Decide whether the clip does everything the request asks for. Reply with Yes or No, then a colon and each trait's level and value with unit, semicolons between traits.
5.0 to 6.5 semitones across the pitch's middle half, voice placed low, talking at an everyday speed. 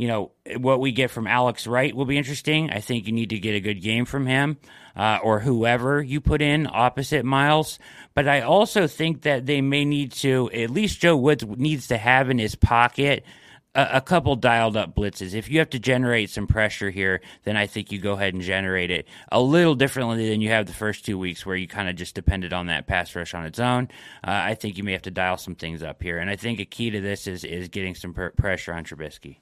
No: wide, 5.6 semitones; low, 115 Hz; fast, 250 wpm